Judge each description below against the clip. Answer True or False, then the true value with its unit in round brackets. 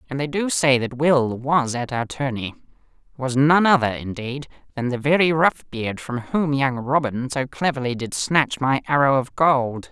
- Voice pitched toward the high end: False (135 Hz)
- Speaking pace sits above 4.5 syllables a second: False (4.4 syllables/s)